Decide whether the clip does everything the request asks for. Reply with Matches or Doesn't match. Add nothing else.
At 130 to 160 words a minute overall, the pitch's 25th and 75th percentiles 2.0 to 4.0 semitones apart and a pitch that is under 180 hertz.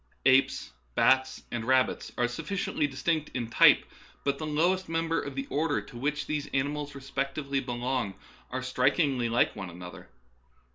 Matches